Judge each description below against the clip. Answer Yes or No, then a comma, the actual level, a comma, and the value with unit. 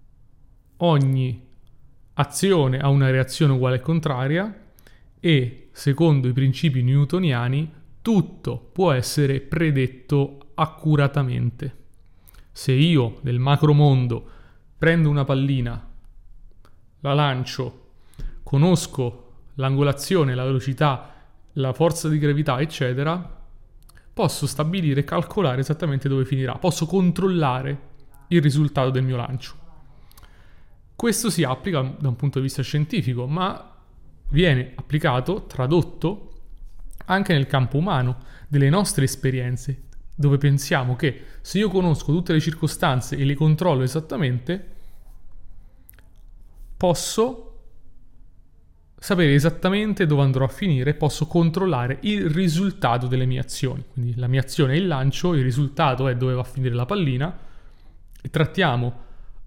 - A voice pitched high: No, medium, 140 Hz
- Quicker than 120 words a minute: No, slow, 115 wpm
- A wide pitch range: No, average, 4.3 semitones